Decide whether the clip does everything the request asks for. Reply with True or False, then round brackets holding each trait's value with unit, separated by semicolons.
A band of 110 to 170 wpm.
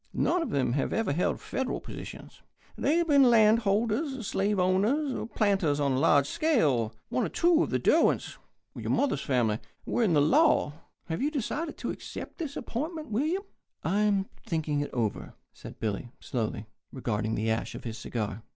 False (180 wpm)